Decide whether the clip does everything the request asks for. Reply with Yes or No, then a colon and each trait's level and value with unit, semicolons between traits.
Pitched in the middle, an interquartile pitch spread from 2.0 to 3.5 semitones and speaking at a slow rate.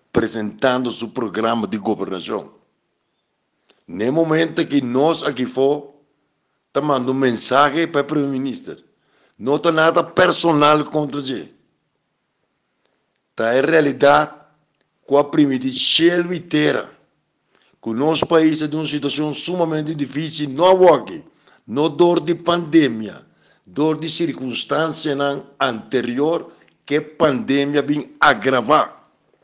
Yes: medium, 150 Hz; average, 2.7 semitones; slow, 120 wpm